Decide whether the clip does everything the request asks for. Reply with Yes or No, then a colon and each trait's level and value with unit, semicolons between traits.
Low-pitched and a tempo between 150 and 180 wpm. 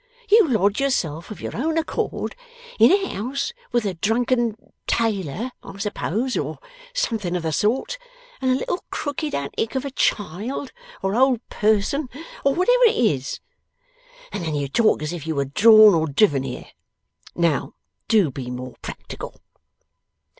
No: high, 215 Hz; average, 155 wpm